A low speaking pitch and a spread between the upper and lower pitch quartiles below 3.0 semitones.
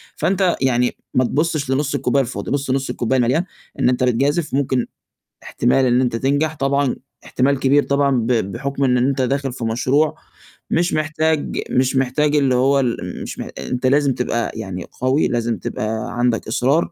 Yes: low, 130 Hz; narrow, 2.4 semitones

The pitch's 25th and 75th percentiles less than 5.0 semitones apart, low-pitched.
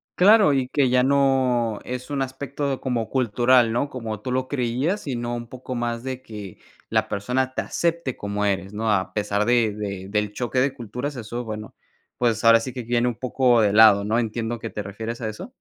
Yes: average, 3.2 semitones; low, 120 Hz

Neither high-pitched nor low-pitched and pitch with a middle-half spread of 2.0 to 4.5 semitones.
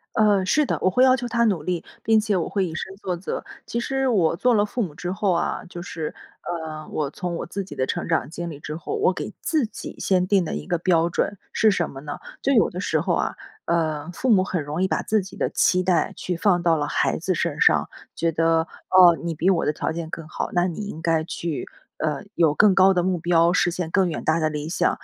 Yes: medium, 175 Hz; average, 3.3 semitones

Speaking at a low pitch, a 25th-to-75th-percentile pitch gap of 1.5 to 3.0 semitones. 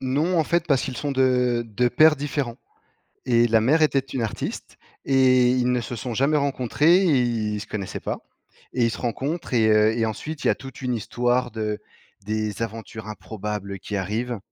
No: low, 125 Hz; average, 3.5 semitones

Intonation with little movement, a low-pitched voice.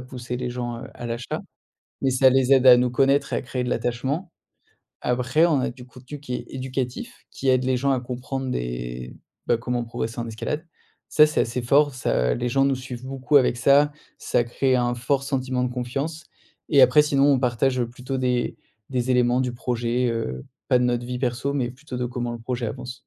Yes: narrow, 1.7 semitones; low, 125 Hz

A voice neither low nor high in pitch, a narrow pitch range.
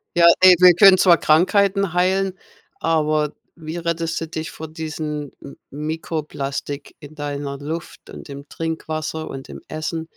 Yes: medium, 160 Hz; narrow, 2.2 semitones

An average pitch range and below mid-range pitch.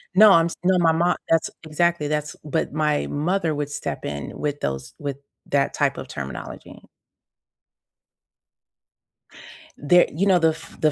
No: average, 3.0 semitones; medium, 155 Hz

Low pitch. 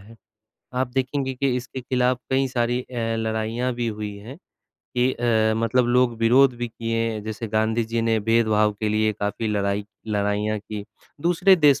Yes: low, 115 Hz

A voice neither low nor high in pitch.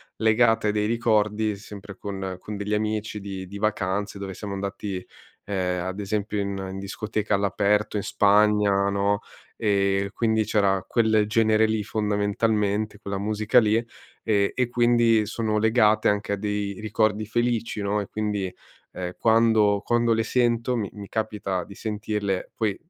No: low, 105 Hz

